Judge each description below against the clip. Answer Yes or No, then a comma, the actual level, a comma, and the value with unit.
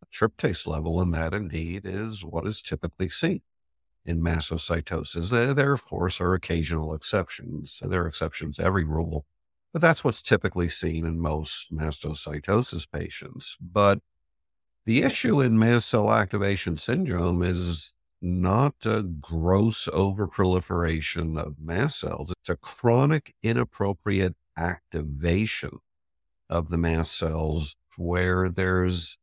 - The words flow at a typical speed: No, slow, 125 wpm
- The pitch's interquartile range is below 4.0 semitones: Yes, average, 3.6 semitones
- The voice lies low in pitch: Yes, very low, 85 Hz